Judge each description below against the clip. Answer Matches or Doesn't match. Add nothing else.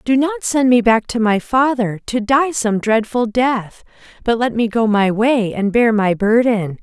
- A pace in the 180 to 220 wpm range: Matches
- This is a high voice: Matches